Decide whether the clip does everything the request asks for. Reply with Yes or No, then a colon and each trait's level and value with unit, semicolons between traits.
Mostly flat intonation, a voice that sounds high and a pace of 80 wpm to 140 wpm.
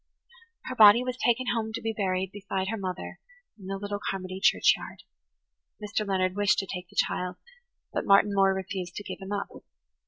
No: narrow, 1.8 semitones; high, 195 Hz; average, 185 wpm